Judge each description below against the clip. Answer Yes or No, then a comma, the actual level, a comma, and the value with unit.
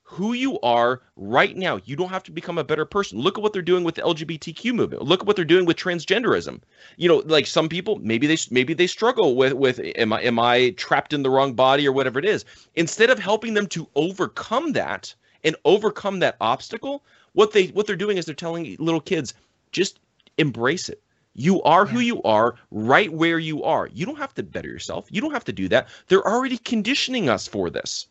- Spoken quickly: Yes, fast, 225 wpm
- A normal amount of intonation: No, wide, 5.9 semitones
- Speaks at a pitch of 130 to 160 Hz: No, medium, 170 Hz